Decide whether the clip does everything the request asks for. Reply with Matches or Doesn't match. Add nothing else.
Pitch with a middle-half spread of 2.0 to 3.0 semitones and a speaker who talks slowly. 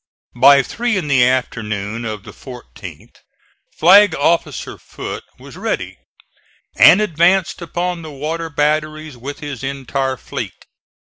Doesn't match